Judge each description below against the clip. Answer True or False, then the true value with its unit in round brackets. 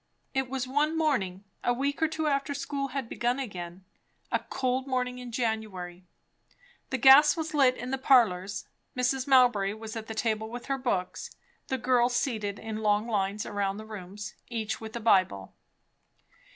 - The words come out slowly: False (170 wpm)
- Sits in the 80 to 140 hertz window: False (240 Hz)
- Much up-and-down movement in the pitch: False (4.3 semitones)